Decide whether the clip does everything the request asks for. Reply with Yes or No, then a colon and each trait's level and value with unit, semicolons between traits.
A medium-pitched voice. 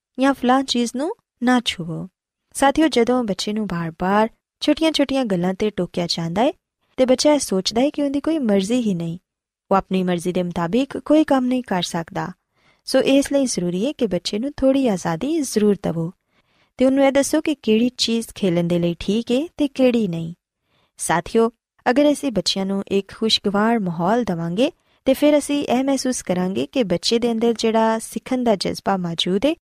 No: high, 230 Hz